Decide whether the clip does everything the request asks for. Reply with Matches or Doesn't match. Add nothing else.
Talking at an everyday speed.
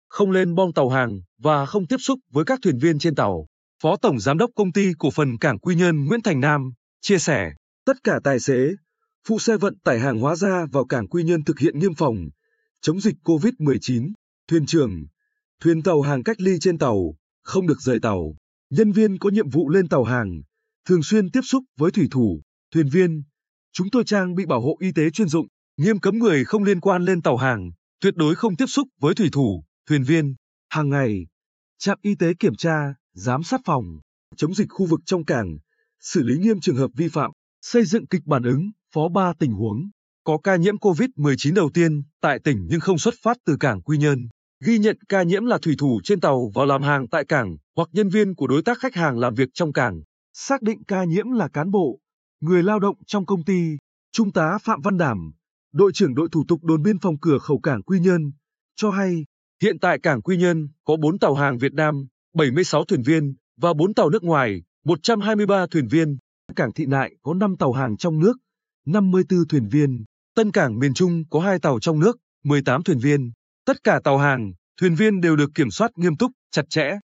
Matches